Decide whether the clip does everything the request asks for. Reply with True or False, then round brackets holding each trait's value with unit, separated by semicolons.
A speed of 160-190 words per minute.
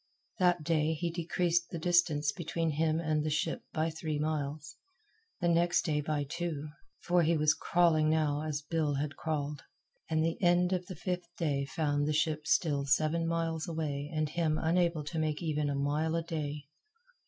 True (180 wpm)